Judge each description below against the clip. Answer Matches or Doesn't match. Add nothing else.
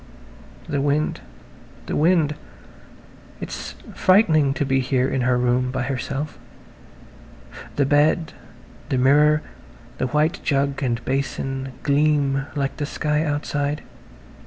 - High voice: Doesn't match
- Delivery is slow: Matches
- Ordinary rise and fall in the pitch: Doesn't match